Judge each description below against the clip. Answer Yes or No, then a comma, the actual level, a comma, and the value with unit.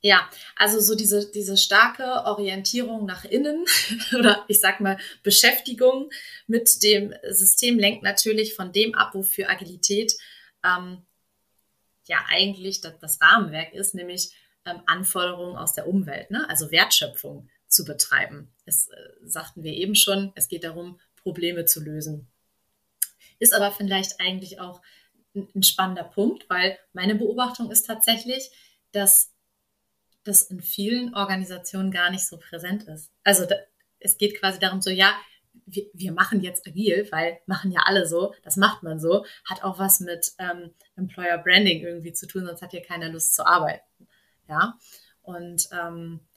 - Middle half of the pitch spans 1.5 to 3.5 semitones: Yes, average, 2.9 semitones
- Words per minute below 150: No, average, 155 wpm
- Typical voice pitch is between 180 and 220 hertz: Yes, high, 190 Hz